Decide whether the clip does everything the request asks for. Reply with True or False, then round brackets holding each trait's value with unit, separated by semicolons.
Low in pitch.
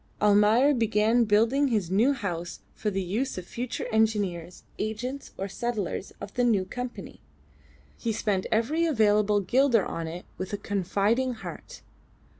False (215 Hz)